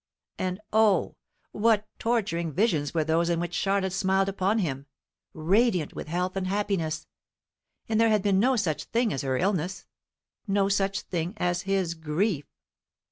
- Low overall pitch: No, high, 190 Hz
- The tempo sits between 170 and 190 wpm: No, average, 155 wpm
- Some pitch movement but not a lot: Yes, average, 3.5 semitones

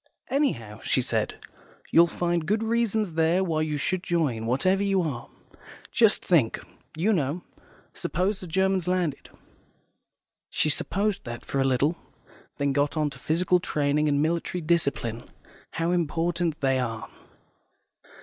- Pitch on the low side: No, medium, 165 Hz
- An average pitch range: Yes, average, 4.4 semitones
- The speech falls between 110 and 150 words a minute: Yes, average, 140 wpm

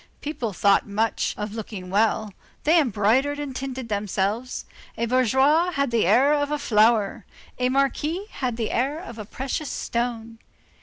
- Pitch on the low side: No, high, 240 Hz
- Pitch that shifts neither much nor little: Yes, average, 4.5 semitones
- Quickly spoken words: No, average, 155 wpm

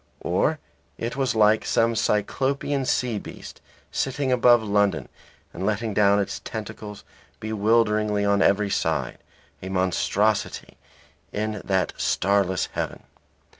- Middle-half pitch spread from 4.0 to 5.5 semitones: No, narrow, 2.5 semitones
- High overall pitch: No, low, 105 Hz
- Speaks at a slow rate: Yes, slow, 115 wpm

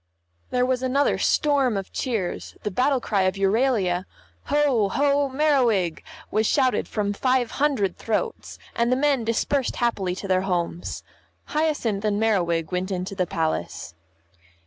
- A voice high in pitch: Yes, high, 225 Hz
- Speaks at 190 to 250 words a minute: No, average, 145 wpm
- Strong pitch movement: Yes, wide, 5.9 semitones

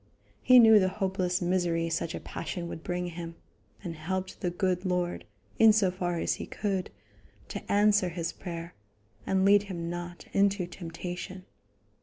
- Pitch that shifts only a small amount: Yes, narrow, 1.9 semitones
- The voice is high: No, medium, 180 Hz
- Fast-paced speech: No, average, 160 wpm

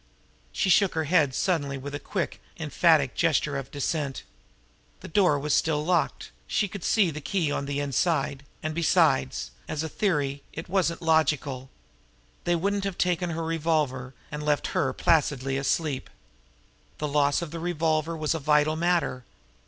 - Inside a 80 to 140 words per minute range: No, average, 160 wpm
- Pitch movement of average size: Yes, average, 3.0 semitones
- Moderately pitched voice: Yes, medium, 155 Hz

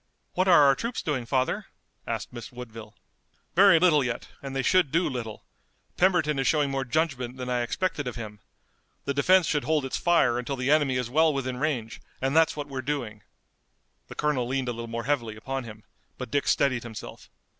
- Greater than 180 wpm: Yes, average, 200 wpm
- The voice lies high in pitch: No, low, 135 Hz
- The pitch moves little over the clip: No, average, 3.7 semitones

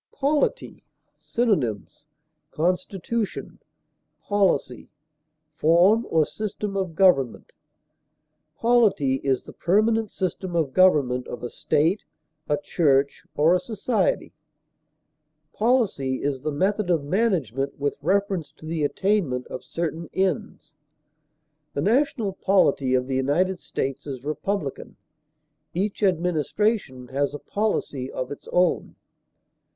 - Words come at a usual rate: No, slow, 110 wpm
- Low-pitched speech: No, medium, 170 Hz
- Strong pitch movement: Yes, wide, 6.2 semitones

